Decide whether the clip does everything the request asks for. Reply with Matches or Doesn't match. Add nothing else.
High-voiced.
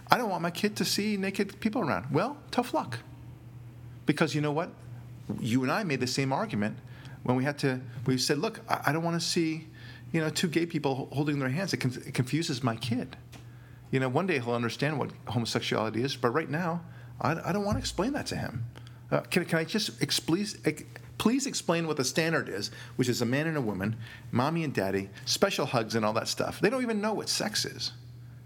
Doesn't match